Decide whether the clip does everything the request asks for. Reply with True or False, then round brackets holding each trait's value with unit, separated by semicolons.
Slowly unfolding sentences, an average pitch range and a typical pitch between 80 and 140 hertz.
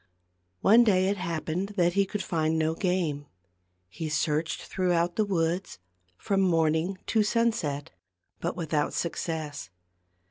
False (130 wpm; 3.5 semitones; 170 Hz)